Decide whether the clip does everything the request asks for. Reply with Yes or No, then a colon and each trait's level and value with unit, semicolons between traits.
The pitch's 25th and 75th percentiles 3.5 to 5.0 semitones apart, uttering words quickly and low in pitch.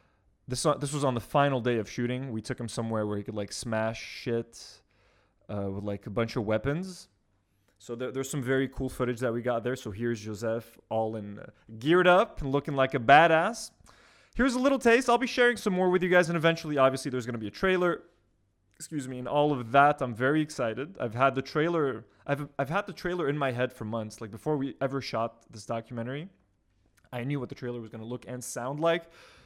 Yes: average, 4.7 semitones; fast, 230 wpm; low, 125 Hz